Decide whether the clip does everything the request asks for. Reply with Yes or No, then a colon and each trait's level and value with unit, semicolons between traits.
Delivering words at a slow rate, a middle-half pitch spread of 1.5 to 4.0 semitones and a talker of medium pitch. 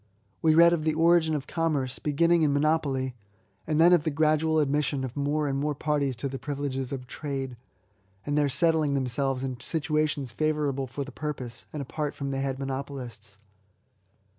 No: average, 180 wpm; narrow, 2.5 semitones; medium, 145 Hz